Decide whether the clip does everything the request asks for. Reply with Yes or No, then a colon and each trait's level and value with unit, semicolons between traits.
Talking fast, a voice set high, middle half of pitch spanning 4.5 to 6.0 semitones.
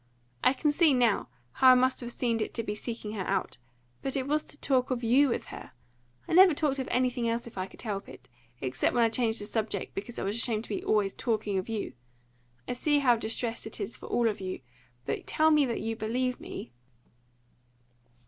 No: fast, 220 wpm; high, 235 Hz; average, 3.1 semitones